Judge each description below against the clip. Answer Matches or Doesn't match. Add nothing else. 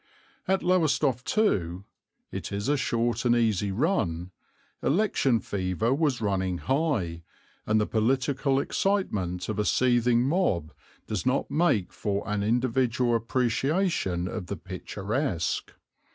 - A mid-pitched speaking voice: Doesn't match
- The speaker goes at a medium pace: Doesn't match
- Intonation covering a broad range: Matches